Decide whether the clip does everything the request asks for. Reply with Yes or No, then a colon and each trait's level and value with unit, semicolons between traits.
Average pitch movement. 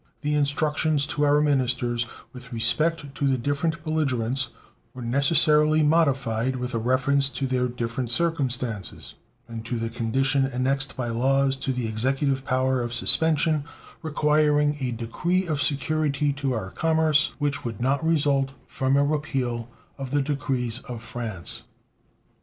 Yes: average, 3.1 semitones